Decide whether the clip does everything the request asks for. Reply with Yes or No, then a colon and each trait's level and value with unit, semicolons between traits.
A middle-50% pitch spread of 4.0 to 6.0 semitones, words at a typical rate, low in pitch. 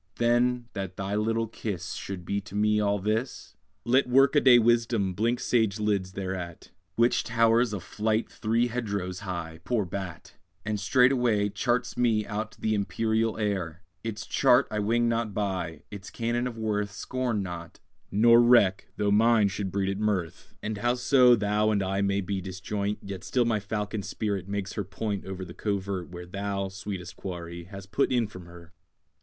No: average, 3.0 semitones; average, 170 wpm; low, 105 Hz